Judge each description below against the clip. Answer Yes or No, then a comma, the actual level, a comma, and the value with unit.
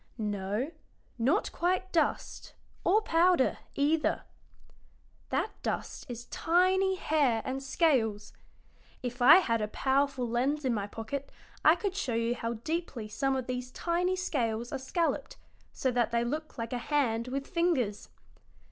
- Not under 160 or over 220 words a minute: No, average, 145 wpm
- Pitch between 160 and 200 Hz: No, very high, 265 Hz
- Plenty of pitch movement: Yes, wide, 5.9 semitones